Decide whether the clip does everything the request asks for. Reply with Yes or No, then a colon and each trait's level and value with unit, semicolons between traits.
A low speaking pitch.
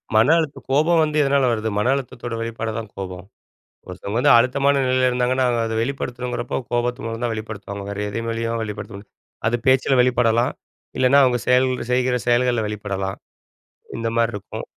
Yes: low, 120 Hz